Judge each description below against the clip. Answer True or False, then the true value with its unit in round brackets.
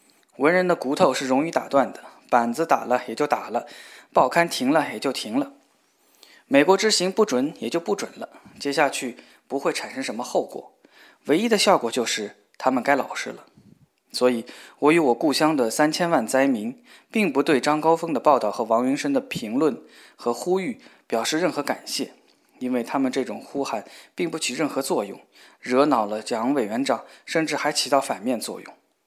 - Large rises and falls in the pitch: True (6.6 semitones)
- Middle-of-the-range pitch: True (150 Hz)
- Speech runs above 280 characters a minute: False (270 characters per minute)